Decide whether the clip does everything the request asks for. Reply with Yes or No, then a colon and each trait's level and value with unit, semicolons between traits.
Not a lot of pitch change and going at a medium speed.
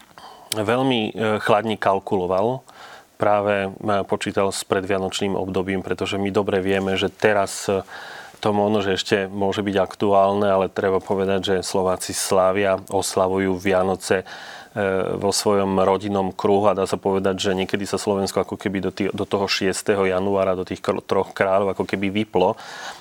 Yes: narrow, 1.4 semitones; average, 145 wpm